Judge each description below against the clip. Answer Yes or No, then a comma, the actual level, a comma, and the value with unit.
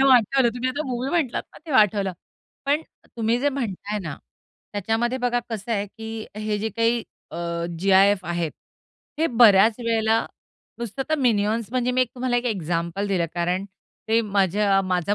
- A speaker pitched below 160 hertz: No, high, 220 Hz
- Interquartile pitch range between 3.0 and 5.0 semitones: Yes, average, 3.6 semitones